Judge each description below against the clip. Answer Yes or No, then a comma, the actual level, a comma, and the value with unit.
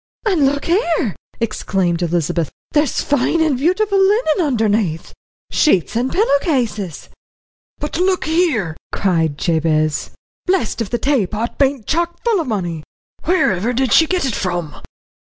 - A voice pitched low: No, very high, 250 Hz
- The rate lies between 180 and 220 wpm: No, slow, 135 wpm